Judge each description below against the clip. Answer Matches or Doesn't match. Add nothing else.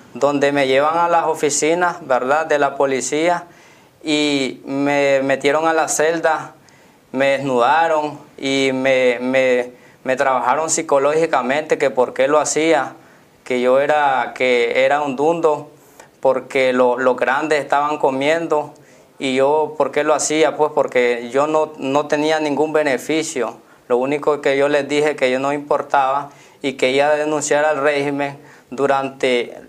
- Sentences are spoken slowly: Doesn't match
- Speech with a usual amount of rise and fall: Doesn't match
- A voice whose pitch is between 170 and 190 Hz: Doesn't match